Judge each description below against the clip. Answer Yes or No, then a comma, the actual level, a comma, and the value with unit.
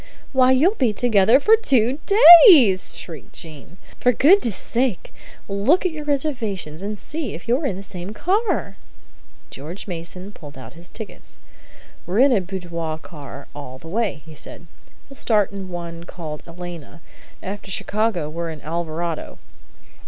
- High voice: Yes, high, 195 Hz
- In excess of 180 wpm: No, average, 150 wpm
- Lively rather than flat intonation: Yes, wide, 7.1 semitones